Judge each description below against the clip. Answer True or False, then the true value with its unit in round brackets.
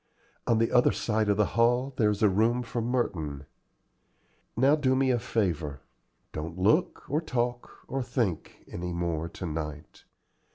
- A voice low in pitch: True (110 Hz)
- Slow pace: False (160 wpm)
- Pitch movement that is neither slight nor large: False (6.1 semitones)